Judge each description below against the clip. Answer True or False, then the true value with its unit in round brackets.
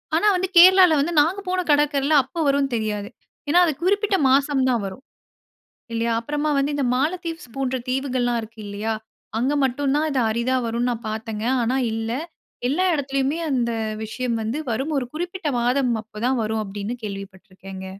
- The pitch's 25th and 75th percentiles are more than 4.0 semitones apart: True (4.9 semitones)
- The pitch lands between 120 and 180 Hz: False (260 Hz)